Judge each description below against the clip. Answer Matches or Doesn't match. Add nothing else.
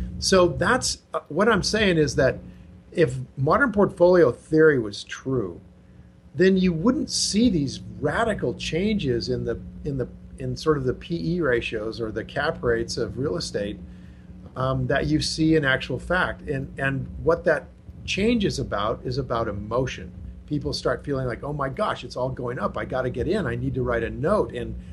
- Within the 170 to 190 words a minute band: Matches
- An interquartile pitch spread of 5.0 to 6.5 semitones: Matches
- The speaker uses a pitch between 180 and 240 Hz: Doesn't match